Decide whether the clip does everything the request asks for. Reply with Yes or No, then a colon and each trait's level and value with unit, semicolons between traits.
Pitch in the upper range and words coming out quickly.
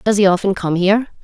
Yes: high, 195 Hz; fast, 245 wpm